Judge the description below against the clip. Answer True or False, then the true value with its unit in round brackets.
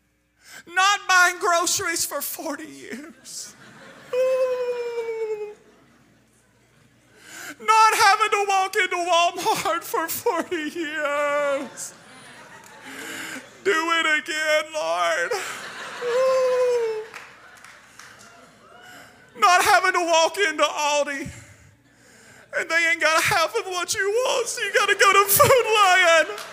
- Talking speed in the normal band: False (95 wpm)